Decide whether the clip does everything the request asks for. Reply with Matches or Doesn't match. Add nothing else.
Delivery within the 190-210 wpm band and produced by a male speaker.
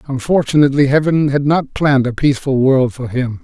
Doesn't match